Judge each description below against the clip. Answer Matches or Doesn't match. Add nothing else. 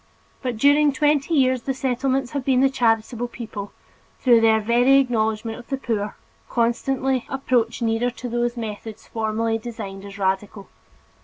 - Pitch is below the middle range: Doesn't match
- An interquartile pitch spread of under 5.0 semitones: Matches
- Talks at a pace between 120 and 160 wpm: Matches